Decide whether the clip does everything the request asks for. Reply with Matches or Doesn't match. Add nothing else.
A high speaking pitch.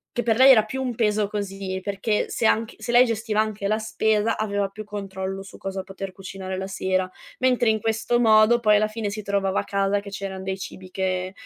Matches